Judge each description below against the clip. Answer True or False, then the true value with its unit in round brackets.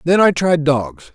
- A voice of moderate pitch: True (165 Hz)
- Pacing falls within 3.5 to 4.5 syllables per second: True (3.9 syllables/s)